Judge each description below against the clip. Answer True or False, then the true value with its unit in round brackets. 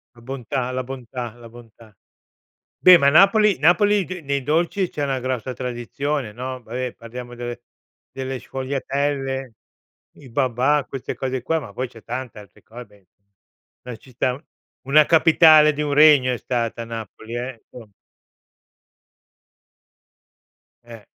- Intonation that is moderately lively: True (3.1 semitones)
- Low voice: True (130 Hz)